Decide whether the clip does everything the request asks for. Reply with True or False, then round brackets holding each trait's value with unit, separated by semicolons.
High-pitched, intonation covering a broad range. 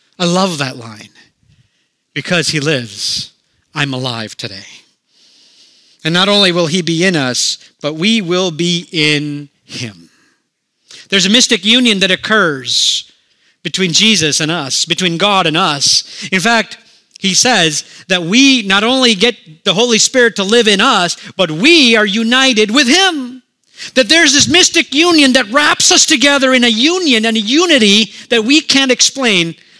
True (200 Hz; 7.2 semitones)